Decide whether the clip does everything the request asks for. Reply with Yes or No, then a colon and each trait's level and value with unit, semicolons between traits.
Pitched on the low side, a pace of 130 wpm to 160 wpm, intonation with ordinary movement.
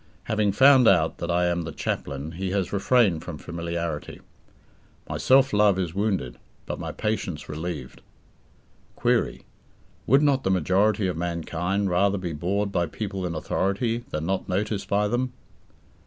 Yes: very low, 95 Hz; average, 155 wpm; average, 3.7 semitones